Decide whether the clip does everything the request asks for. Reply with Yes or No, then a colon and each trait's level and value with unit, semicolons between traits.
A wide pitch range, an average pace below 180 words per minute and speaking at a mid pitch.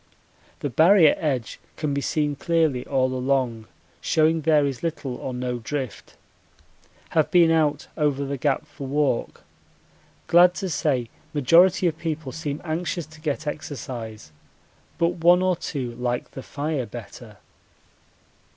No: average, 3.8 semitones; average, 140 wpm; medium, 145 Hz